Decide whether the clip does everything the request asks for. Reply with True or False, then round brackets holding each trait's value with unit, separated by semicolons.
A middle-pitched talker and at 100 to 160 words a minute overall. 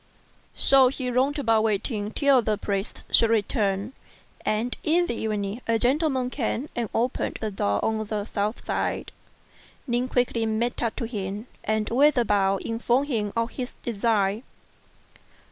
False (230 Hz; 155 wpm)